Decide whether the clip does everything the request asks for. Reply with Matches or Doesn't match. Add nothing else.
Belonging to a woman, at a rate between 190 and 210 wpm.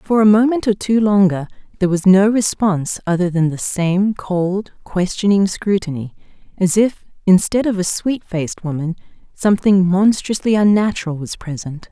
Doesn't match